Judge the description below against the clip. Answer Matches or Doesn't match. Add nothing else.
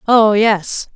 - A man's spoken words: Doesn't match